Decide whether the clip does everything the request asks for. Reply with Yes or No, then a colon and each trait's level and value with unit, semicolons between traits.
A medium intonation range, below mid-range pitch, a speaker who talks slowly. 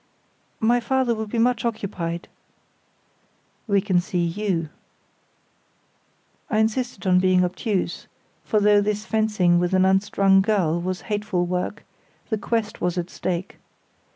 No: average, 3.3 semitones; high, 195 Hz; slow, 130 wpm